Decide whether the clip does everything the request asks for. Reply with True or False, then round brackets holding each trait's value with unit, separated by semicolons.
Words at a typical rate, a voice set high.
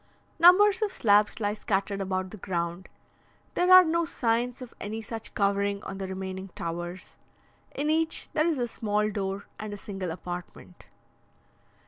True (155 wpm; 205 Hz)